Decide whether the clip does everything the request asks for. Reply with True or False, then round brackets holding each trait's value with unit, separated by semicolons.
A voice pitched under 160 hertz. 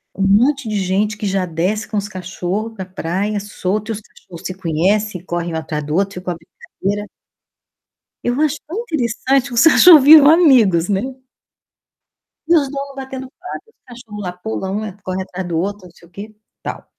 False (205 Hz)